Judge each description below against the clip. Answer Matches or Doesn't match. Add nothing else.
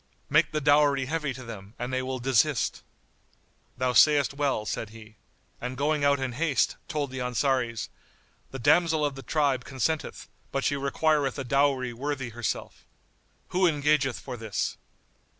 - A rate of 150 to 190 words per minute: Matches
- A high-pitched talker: Doesn't match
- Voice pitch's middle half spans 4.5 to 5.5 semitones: Doesn't match